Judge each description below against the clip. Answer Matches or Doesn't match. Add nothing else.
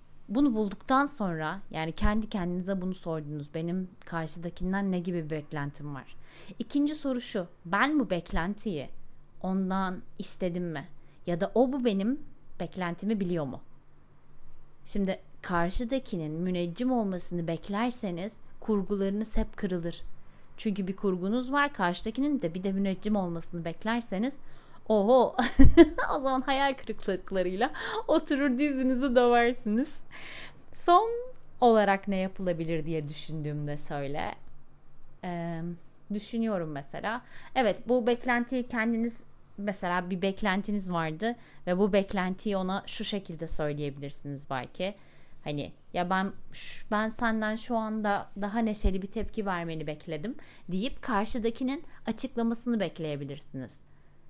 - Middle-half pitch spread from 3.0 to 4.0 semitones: Doesn't match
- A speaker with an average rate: Matches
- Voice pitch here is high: Matches